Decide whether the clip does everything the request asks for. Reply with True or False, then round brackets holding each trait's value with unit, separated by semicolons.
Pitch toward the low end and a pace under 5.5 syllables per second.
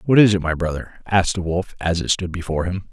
False (90 Hz; 6.1 syllables/s)